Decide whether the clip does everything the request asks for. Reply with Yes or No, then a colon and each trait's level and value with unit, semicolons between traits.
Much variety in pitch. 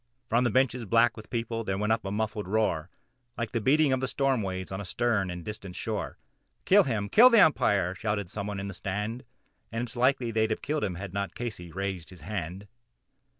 No: average, 3.7 semitones